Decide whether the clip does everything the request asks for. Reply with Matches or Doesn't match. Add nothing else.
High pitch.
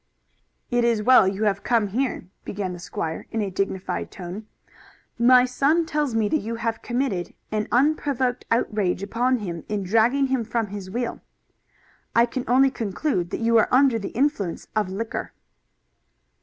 Matches